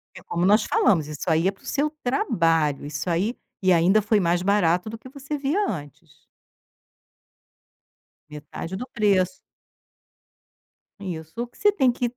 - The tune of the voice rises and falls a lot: Yes, wide, 6.4 semitones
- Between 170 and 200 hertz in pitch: Yes, high, 190 Hz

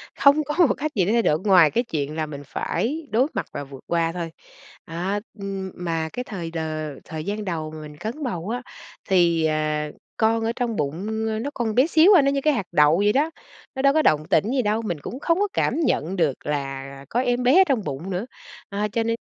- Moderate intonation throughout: No, wide, 7.6 semitones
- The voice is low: No, high, 200 Hz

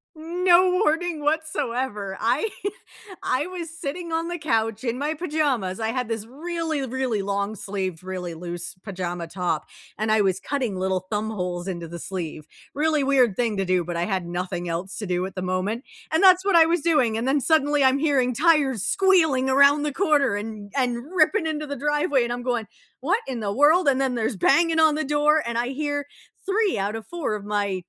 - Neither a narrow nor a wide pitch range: No, wide, 7.4 semitones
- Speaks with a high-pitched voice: Yes, very high, 255 Hz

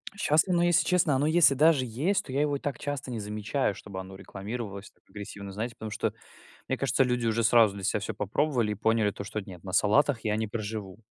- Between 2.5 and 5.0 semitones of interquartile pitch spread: No, wide, 5.6 semitones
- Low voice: Yes, low, 115 Hz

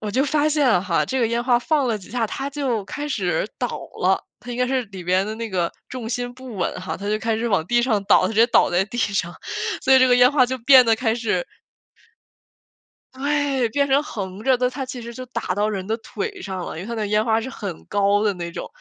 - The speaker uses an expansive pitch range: No, average, 4.1 semitones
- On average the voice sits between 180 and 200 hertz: No, high, 230 Hz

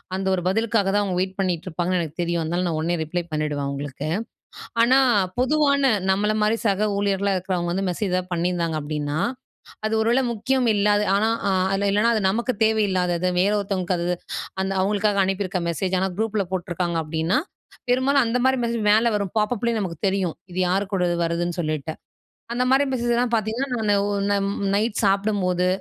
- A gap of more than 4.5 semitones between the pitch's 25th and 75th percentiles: No, average, 3.8 semitones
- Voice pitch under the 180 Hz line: No, high, 195 Hz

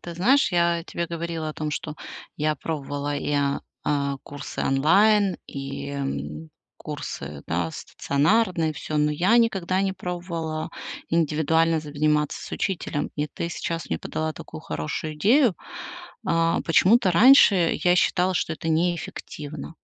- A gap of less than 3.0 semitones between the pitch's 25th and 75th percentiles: No, average, 3.3 semitones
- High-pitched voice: No, medium, 160 Hz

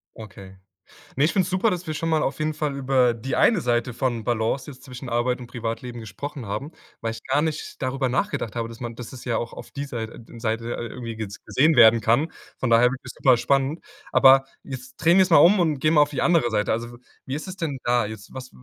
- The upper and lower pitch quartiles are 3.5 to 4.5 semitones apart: Yes, average, 4.1 semitones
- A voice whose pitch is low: Yes, low, 130 Hz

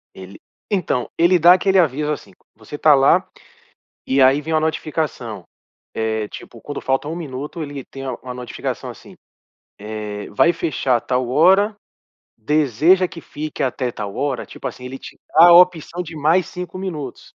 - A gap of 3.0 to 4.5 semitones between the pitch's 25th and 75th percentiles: No, average, 4.9 semitones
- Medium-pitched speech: Yes, medium, 145 Hz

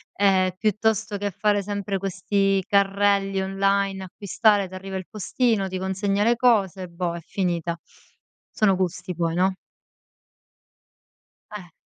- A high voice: Yes, high, 195 Hz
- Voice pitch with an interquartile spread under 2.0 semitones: Yes, narrow, 1.5 semitones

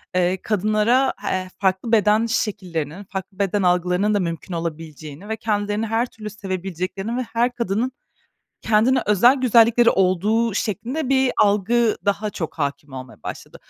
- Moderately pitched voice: No, high, 205 Hz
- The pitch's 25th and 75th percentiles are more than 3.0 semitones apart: Yes, average, 3.8 semitones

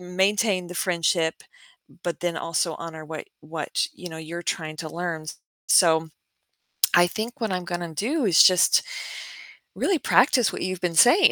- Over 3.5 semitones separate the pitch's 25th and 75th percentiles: No, average, 2.7 semitones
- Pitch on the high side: No, medium, 175 Hz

